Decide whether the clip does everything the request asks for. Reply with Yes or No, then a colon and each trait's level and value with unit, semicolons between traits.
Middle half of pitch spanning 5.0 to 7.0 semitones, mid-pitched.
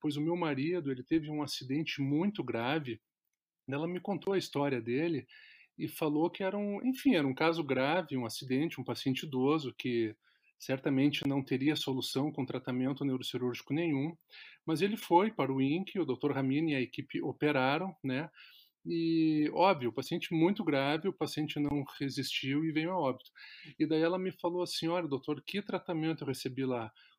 No: average, 3.8 semitones; medium, 150 Hz